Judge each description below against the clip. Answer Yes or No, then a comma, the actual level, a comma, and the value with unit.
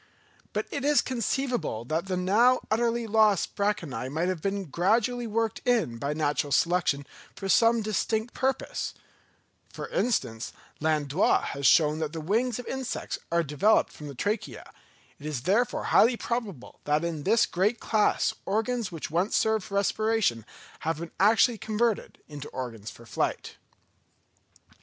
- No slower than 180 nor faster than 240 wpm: No, average, 150 wpm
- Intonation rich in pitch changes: Yes, wide, 6.9 semitones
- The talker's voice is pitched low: No, high, 200 Hz